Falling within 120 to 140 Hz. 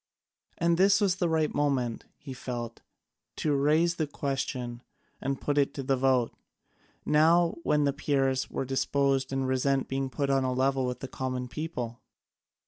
Yes: low, 135 Hz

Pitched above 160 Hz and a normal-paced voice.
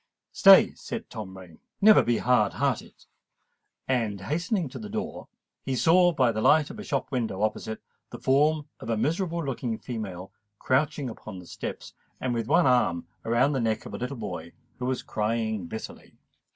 No: low, 125 Hz; average, 180 wpm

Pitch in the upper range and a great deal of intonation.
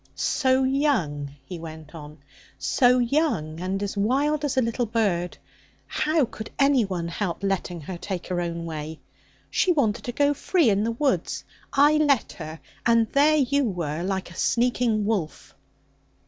Yes: high, 215 Hz; wide, 7.9 semitones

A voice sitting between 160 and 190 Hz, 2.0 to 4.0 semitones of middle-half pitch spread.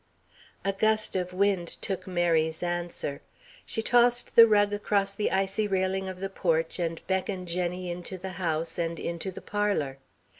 Yes: medium, 185 Hz; narrow, 2.5 semitones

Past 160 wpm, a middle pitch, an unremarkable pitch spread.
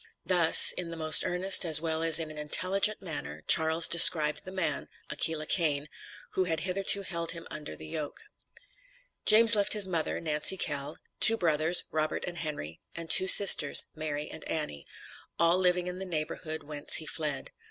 Yes: average, 175 wpm; medium, 165 Hz; average, 3.0 semitones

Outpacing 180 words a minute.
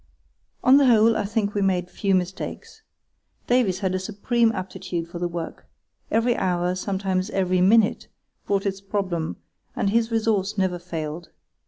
No: average, 155 wpm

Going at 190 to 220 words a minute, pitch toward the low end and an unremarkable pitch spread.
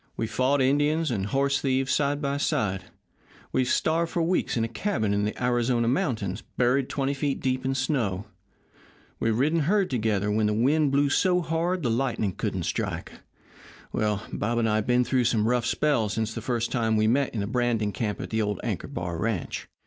Yes: average, 200 wpm; low, 125 Hz; average, 4.4 semitones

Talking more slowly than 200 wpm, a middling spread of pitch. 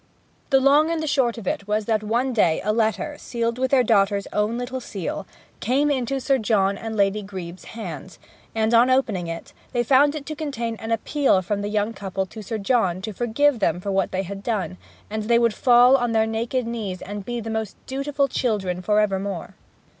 No: fast, 205 wpm; average, 4.0 semitones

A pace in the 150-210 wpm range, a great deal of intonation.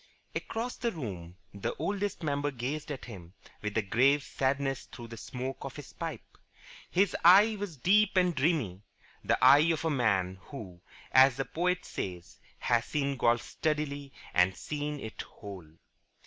Yes: average, 160 wpm; wide, 6.3 semitones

